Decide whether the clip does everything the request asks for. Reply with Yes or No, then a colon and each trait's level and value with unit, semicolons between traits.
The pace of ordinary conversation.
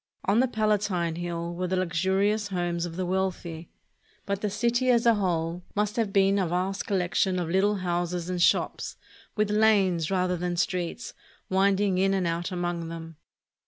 Yes: average, 170 wpm